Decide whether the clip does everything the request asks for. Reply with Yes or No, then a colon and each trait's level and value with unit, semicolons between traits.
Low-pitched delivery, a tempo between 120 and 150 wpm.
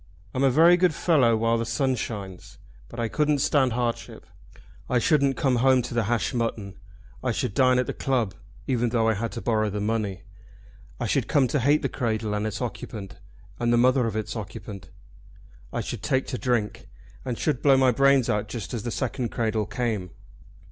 No: low, 120 Hz; average, 200 wpm